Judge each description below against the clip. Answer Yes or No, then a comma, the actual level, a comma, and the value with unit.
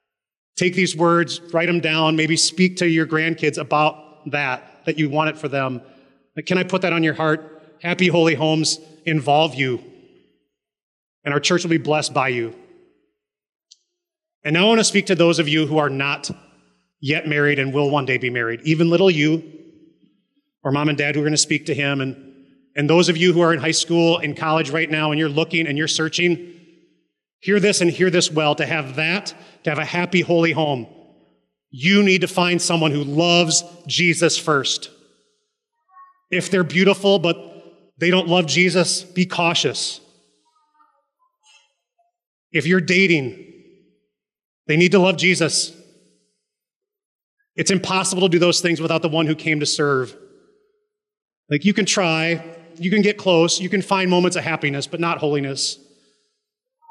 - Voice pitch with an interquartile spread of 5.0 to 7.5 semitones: No, average, 3.5 semitones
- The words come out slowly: No, average, 175 wpm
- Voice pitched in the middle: Yes, medium, 165 Hz